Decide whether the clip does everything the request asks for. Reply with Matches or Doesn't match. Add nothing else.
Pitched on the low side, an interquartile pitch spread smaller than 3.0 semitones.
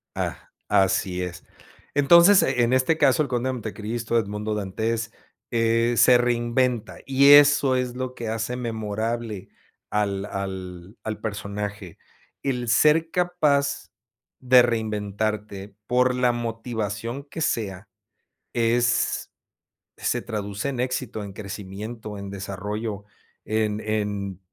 Doesn't match